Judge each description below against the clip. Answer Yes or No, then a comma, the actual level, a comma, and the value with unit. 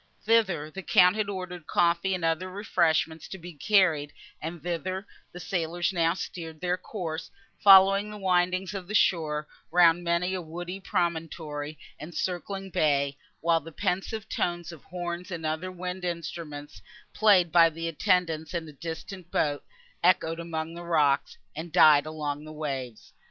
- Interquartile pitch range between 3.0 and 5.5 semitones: No, narrow, 2.6 semitones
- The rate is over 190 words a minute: No, average, 155 wpm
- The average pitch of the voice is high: No, medium, 170 Hz